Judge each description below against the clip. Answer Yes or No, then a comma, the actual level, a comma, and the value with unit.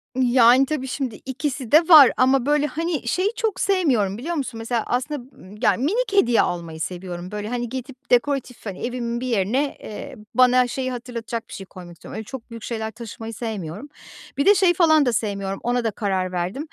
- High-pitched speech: Yes, high, 245 Hz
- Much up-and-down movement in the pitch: No, average, 4.2 semitones